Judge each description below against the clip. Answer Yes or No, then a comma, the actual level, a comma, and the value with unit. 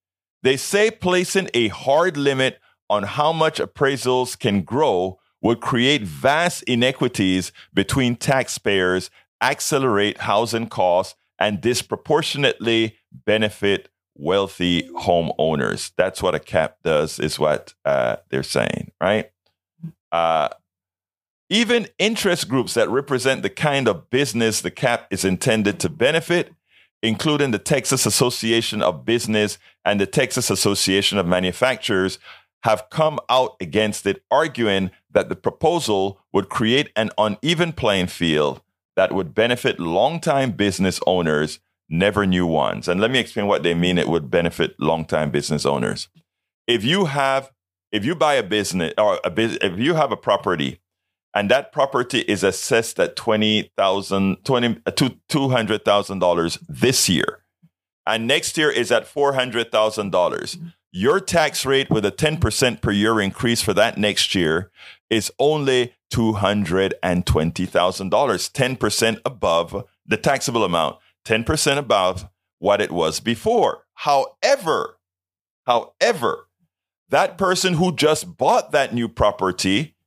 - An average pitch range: No, wide, 6.3 semitones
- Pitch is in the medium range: No, low, 110 Hz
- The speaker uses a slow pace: Yes, slow, 130 wpm